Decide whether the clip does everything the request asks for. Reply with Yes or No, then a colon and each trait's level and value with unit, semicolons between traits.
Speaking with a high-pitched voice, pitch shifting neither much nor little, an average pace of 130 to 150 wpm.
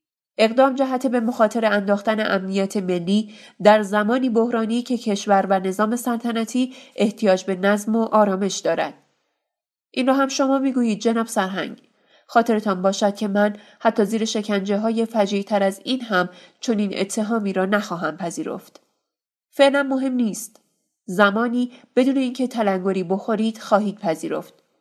Yes: high, 215 Hz; average, 3.3 semitones; average, 135 wpm